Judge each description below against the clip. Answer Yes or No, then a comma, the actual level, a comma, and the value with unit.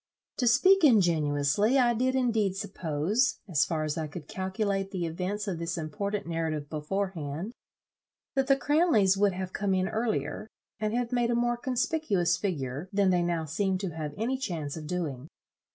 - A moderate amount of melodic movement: No, wide, 5.9 semitones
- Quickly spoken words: No, average, 175 wpm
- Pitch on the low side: No, high, 190 Hz